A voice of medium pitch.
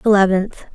No: high, 200 Hz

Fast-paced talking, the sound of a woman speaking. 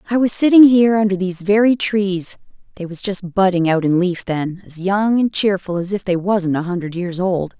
Yes: fast, 215 wpm; female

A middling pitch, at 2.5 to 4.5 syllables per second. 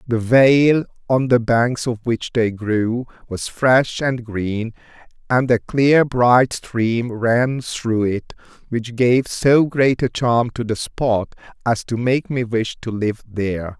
No: low, 120 Hz; 3.3 syllables/s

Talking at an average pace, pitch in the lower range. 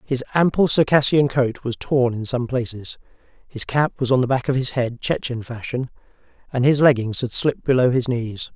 Yes: average, 195 wpm; low, 125 Hz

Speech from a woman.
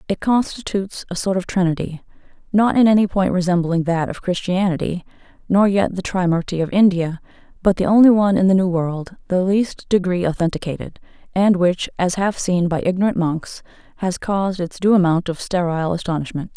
Yes: female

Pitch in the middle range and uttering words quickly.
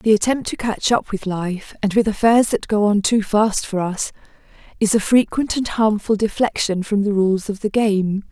No: high, 210 Hz; fast, 210 wpm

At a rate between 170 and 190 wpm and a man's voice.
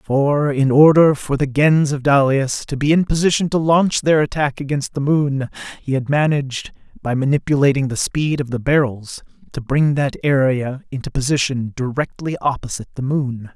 Yes: average, 175 wpm; male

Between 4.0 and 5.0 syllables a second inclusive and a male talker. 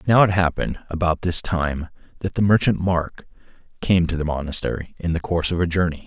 No: 5.8 syllables/s; male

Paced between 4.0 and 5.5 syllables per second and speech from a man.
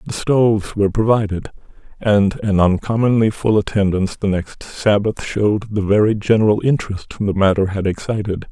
Yes: 5.3 syllables/s; male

